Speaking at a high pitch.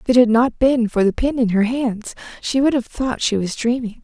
Yes: high, 240 Hz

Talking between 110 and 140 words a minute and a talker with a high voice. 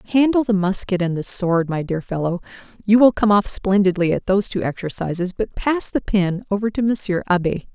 No: average, 200 wpm; high, 195 Hz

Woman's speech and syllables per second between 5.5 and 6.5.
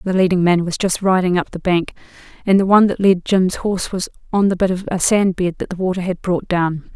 Yes: female; 5.8 syllables/s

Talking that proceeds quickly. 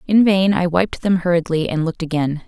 Yes: fast, 220 wpm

